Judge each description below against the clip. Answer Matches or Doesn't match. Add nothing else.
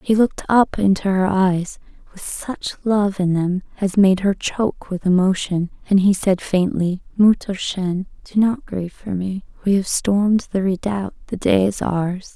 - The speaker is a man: Doesn't match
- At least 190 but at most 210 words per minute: Doesn't match